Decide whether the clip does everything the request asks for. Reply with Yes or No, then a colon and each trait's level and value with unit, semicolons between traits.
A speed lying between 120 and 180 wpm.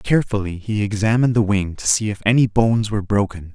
No: fast, 205 wpm